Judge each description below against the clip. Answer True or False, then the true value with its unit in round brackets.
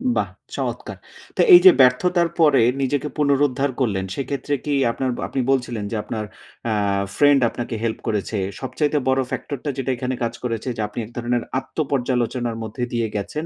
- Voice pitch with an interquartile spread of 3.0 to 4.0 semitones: True (3.4 semitones)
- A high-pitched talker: False (125 Hz)